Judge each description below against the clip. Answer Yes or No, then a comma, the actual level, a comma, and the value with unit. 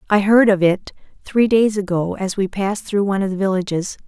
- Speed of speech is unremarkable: No, fast, 220 wpm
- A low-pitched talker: No, high, 200 Hz